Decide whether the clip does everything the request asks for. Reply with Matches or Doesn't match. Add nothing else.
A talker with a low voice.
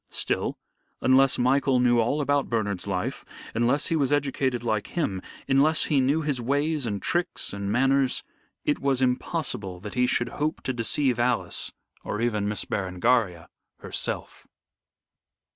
Matches